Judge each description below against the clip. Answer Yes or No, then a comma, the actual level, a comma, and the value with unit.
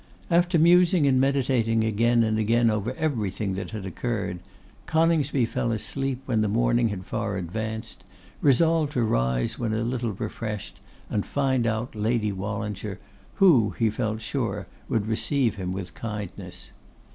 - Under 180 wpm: Yes, average, 145 wpm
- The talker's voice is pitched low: Yes, low, 115 Hz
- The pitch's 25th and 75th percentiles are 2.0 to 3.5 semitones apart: No, average, 3.9 semitones